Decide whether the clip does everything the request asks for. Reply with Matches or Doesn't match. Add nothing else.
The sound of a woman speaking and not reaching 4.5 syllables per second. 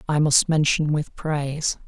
Doesn't match